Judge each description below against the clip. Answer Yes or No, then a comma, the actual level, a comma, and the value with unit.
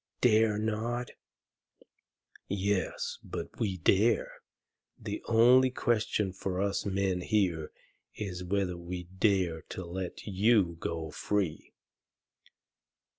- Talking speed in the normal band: No, slow, 100 wpm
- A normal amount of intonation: Yes, average, 3.1 semitones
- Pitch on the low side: Yes, low, 100 Hz